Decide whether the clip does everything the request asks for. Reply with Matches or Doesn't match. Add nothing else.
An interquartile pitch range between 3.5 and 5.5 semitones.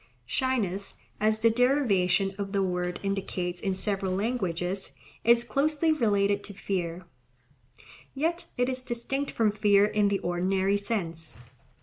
Matches